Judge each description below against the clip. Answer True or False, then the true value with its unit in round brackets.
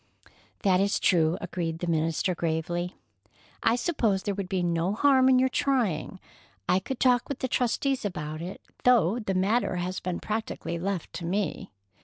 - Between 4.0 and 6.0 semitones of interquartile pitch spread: True (5.6 semitones)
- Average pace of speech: True (170 wpm)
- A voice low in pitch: False (190 Hz)